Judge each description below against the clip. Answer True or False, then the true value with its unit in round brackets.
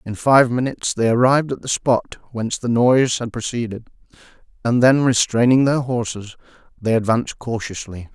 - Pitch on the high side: False (120 Hz)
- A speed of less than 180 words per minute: True (155 wpm)